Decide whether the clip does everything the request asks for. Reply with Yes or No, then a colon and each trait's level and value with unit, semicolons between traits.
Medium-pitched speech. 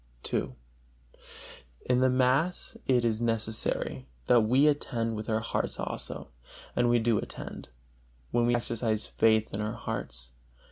No: low, 115 Hz